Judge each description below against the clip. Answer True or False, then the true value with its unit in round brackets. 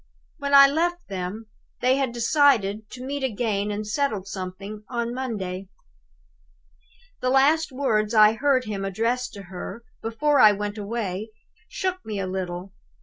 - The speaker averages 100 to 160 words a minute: True (145 wpm)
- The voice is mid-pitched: False (225 Hz)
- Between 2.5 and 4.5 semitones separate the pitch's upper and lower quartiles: False (4.9 semitones)